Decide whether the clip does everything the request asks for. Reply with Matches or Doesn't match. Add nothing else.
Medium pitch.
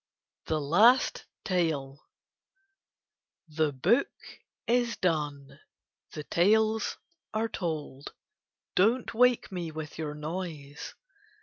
Matches